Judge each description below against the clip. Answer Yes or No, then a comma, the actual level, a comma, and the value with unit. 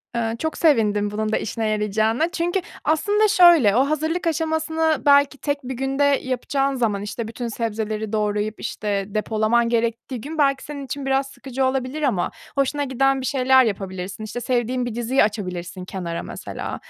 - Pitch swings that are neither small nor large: Yes, average, 4.8 semitones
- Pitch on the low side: No, very high, 250 Hz